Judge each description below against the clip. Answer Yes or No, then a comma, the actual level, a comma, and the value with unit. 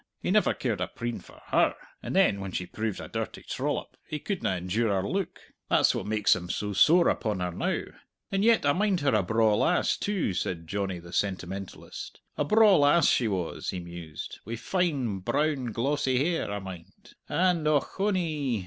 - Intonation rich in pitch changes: Yes, wide, 8.6 semitones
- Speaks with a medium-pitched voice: No, low, 115 Hz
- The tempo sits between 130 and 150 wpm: No, average, 185 wpm